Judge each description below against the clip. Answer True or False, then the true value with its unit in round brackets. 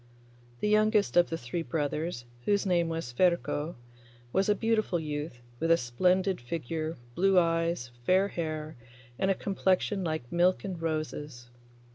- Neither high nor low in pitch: True (170 Hz)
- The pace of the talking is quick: False (145 wpm)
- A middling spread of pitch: True (3.4 semitones)